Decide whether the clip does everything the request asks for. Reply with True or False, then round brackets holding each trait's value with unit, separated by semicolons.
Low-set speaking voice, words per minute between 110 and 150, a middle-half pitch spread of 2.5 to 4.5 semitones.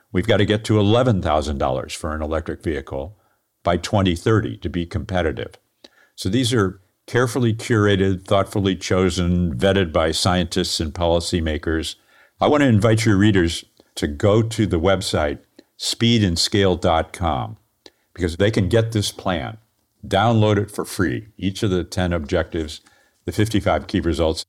True (95 Hz; 140 wpm; 3.6 semitones)